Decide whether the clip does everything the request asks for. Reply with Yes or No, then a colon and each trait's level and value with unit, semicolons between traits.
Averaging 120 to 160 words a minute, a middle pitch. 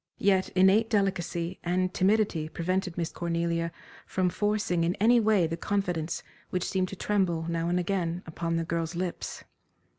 Yes: average, 155 wpm; medium, 180 Hz